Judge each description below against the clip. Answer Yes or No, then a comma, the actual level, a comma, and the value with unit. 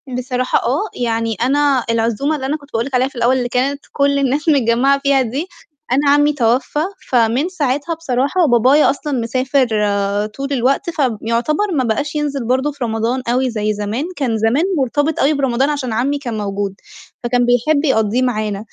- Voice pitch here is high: Yes, very high, 255 Hz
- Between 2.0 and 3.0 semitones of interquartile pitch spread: No, average, 3.5 semitones